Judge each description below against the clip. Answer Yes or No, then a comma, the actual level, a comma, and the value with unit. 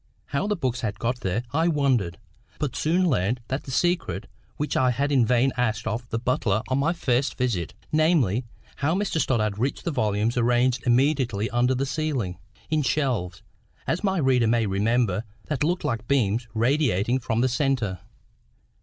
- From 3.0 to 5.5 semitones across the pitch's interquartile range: Yes, average, 4.2 semitones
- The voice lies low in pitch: Yes, low, 125 Hz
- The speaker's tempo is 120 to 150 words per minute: No, average, 165 wpm